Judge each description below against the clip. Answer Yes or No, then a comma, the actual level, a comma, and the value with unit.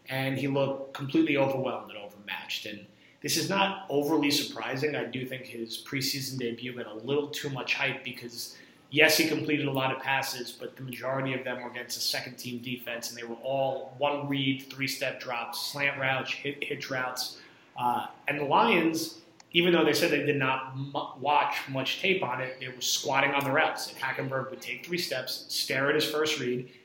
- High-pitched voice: No, low, 135 Hz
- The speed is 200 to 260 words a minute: Yes, fast, 205 wpm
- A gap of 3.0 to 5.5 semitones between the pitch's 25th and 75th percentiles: No, narrow, 2.5 semitones